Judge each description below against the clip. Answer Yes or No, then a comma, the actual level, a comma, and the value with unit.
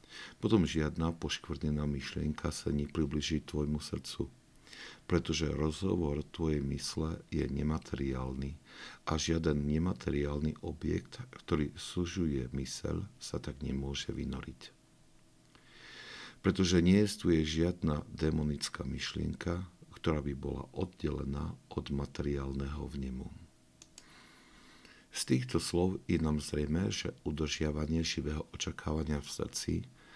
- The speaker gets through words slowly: Yes, slow, 100 wpm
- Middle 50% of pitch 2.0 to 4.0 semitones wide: Yes, average, 2.9 semitones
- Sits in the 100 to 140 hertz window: No, very low, 75 Hz